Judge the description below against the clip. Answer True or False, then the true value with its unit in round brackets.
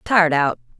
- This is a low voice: False (160 Hz)